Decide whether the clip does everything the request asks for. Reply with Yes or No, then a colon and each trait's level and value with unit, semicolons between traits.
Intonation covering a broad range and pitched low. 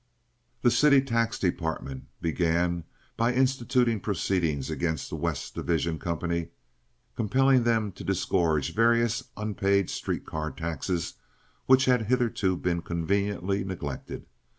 Yes: wide, 5.7 semitones; very low, 95 Hz